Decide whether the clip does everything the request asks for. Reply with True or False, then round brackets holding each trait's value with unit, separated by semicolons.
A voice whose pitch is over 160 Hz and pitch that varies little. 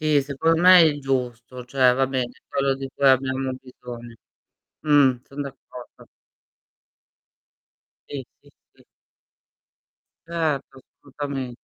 False (135 Hz; 2.2 semitones)